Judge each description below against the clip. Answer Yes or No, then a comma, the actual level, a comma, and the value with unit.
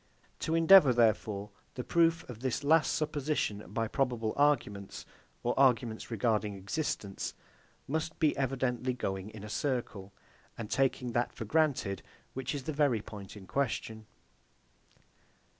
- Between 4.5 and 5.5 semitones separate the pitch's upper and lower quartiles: Yes, average, 5.1 semitones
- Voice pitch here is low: Yes, low, 125 Hz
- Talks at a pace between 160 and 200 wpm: No, slow, 135 wpm